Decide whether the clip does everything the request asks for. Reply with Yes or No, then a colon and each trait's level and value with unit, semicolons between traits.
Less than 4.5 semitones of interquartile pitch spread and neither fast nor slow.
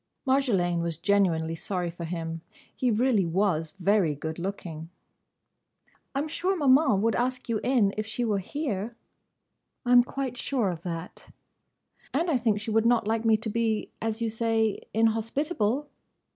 No: average, 5.2 semitones; average, 150 wpm